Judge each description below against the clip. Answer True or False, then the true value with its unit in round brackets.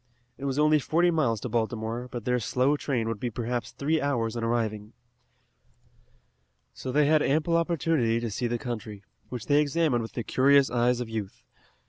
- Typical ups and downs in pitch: True (4.0 semitones)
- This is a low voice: True (125 Hz)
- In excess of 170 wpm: True (180 wpm)